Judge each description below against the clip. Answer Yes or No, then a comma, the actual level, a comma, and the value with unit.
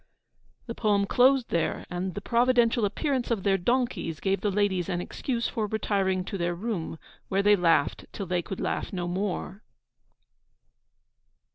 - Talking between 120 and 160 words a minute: Yes, average, 155 wpm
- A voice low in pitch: No, high, 200 Hz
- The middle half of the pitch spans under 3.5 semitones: No, average, 4.3 semitones